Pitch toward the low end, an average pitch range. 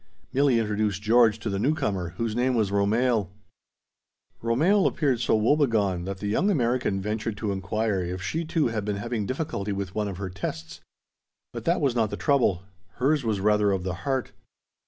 Yes: low, 110 Hz; average, 4.3 semitones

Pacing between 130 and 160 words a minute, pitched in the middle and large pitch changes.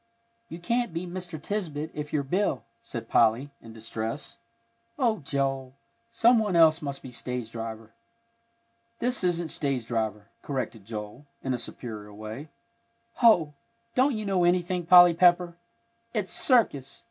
Yes: average, 140 wpm; medium, 150 Hz; wide, 7.3 semitones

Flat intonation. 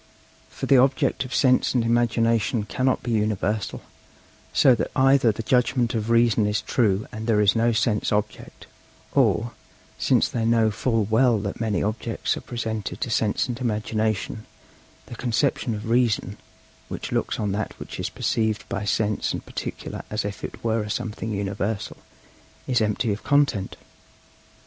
Yes: narrow, 2.1 semitones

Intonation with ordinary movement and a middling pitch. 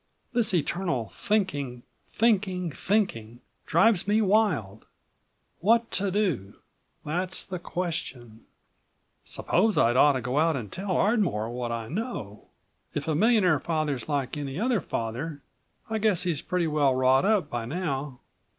No: wide, 7.5 semitones; medium, 160 Hz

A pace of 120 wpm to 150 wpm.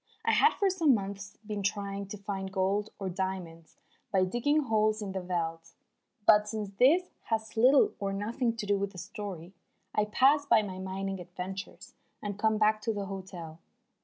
No: average, 180 wpm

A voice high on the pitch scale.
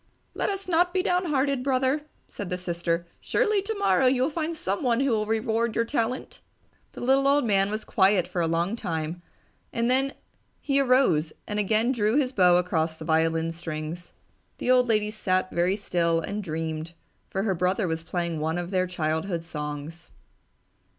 Yes: high, 195 Hz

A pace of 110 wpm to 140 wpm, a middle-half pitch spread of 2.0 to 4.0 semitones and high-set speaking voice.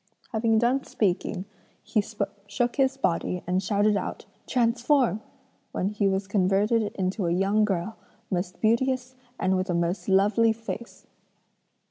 Yes: slow, 135 wpm; average, 3.4 semitones; high, 205 Hz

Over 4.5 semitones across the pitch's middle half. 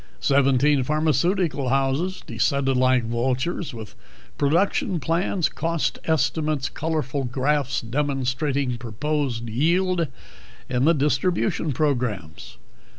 No: average, 3.9 semitones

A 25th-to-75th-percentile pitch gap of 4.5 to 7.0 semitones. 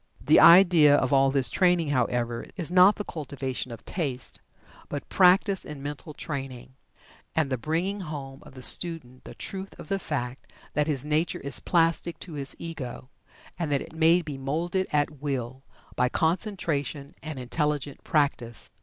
No: average, 3.8 semitones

